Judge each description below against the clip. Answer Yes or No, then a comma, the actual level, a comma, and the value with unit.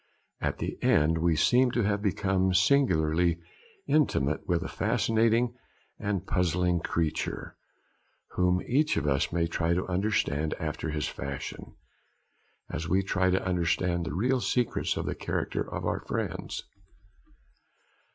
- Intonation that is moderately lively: Yes, average, 3.9 semitones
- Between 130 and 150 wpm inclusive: Yes, slow, 135 wpm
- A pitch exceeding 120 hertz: No, very low, 90 Hz